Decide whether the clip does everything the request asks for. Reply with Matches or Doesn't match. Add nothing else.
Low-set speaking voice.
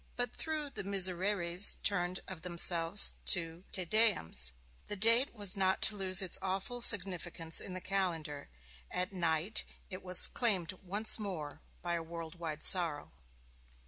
Doesn't match